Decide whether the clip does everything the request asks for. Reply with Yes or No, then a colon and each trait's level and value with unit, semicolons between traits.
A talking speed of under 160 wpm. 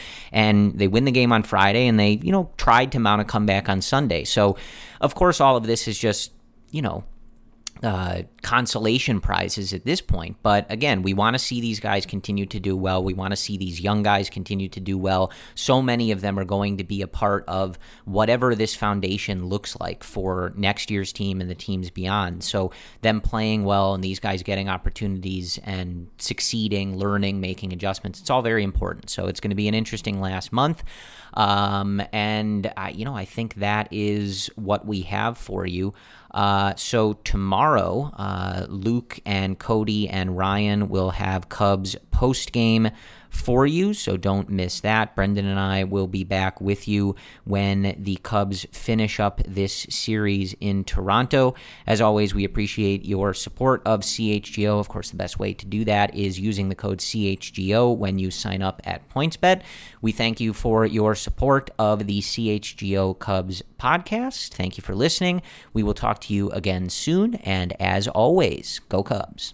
No: average, 185 wpm